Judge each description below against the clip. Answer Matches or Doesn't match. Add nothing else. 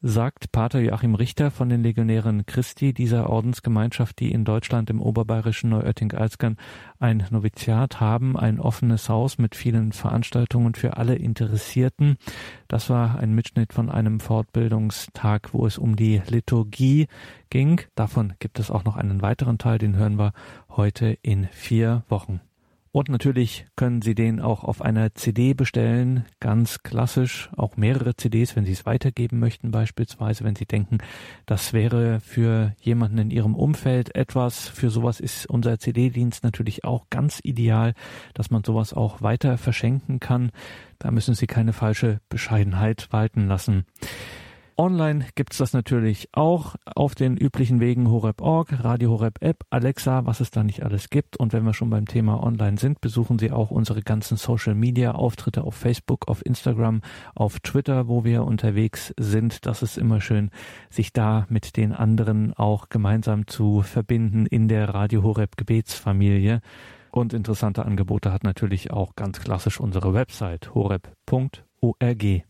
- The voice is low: Matches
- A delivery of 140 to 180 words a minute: Matches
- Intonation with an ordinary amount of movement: Doesn't match